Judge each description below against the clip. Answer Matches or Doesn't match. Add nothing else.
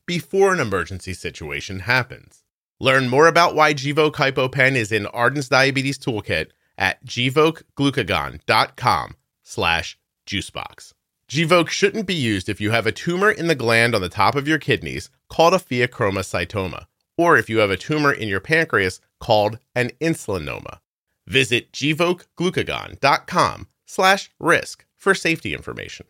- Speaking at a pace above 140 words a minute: Doesn't match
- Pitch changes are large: Matches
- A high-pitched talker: Doesn't match